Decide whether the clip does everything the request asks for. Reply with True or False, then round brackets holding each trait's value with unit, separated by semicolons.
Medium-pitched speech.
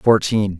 False (105 Hz)